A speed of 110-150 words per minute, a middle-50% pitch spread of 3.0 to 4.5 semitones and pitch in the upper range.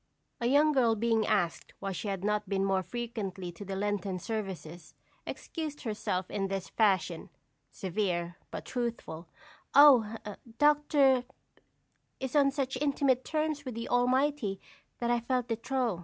No: average, 140 wpm; average, 5.3 semitones; high, 225 Hz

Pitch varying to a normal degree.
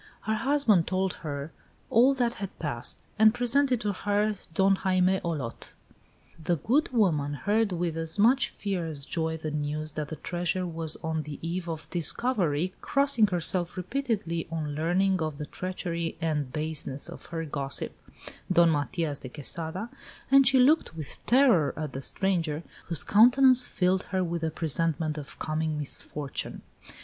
Yes: average, 5.0 semitones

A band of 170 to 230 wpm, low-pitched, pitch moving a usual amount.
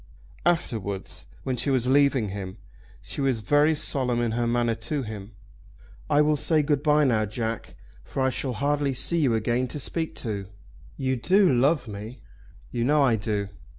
Yes: average, 175 wpm; low, 125 Hz; average, 4.5 semitones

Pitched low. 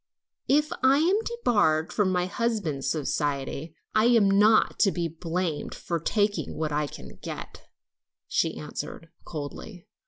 No: medium, 180 Hz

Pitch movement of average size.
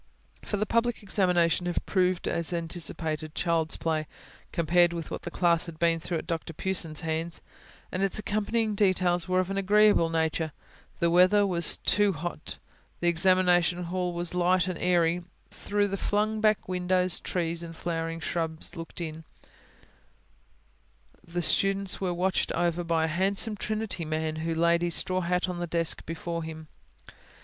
No: narrow, 2.1 semitones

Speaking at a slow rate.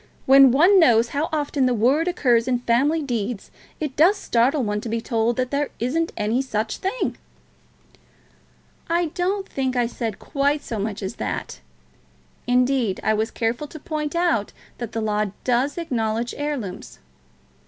No: average, 160 wpm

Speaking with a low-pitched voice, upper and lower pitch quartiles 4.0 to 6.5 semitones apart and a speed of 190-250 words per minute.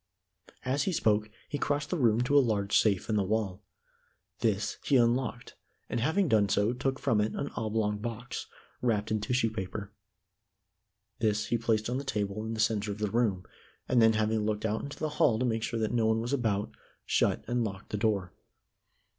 No: low, 110 Hz; average, 2.7 semitones; average, 200 wpm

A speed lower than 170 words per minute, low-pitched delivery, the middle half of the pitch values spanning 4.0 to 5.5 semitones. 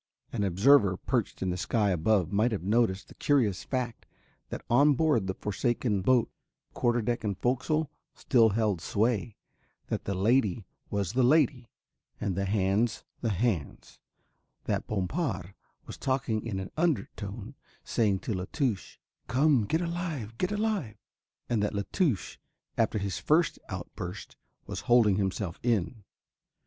Yes: average, 145 wpm; low, 110 Hz; average, 4.8 semitones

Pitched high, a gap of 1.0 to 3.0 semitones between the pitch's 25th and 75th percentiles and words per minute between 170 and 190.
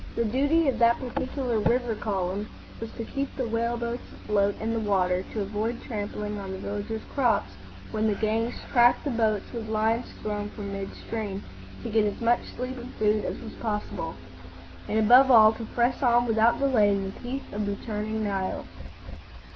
Yes: high, 220 Hz; narrow, 2.5 semitones; average, 185 wpm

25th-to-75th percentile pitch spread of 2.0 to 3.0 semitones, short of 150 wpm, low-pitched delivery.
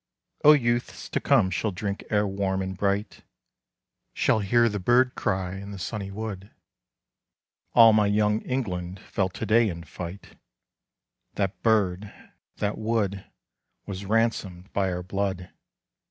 Yes: narrow, 2.6 semitones; average, 140 wpm; low, 100 Hz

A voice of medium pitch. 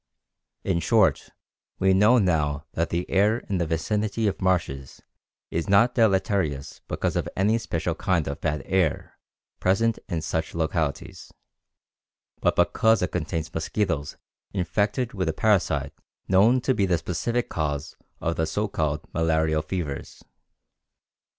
No: very low, 90 Hz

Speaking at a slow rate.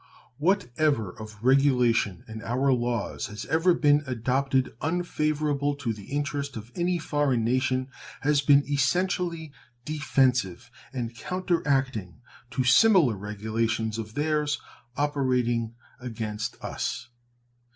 Yes: slow, 110 wpm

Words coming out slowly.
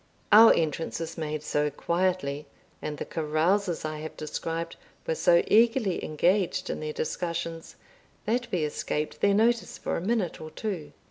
No: average, 155 wpm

